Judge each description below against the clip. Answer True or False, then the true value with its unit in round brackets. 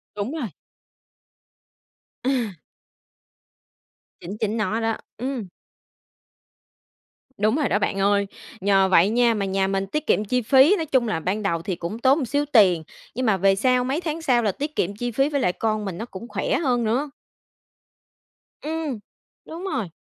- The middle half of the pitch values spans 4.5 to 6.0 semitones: True (5.3 semitones)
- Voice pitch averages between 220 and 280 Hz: True (225 Hz)